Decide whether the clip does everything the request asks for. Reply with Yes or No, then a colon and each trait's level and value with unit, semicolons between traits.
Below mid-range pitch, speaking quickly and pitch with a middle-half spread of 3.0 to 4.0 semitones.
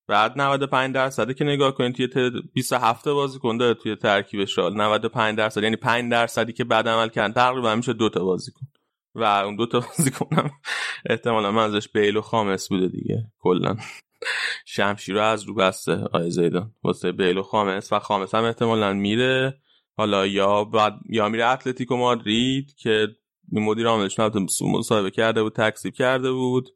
Yes: low, 110 Hz; fast, 165 wpm; average, 3.3 semitones